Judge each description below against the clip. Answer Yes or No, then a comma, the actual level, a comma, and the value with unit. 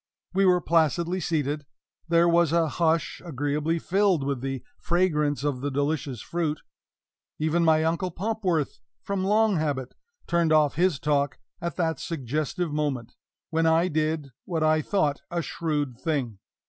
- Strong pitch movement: No, average, 2.9 semitones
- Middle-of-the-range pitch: Yes, medium, 160 Hz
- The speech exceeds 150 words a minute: No, average, 145 wpm